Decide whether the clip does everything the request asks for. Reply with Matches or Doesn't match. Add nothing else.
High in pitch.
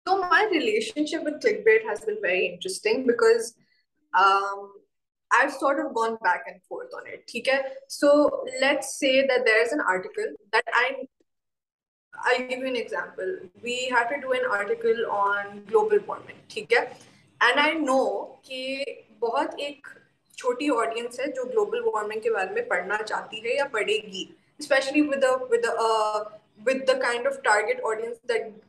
Matches